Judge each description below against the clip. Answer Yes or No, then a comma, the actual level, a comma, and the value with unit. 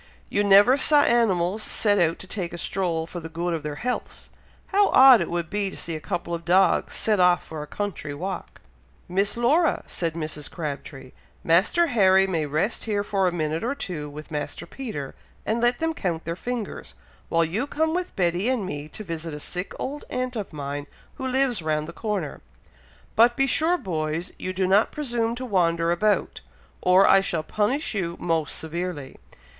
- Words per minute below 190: No, average, 195 wpm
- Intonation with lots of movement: Yes, wide, 5.8 semitones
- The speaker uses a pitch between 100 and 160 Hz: No, medium, 185 Hz